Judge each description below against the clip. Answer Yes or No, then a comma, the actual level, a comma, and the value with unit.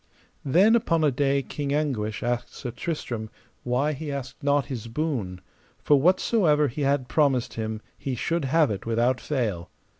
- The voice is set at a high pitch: No, medium, 140 Hz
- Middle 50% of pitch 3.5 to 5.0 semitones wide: Yes, average, 4.2 semitones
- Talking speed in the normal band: Yes, average, 160 wpm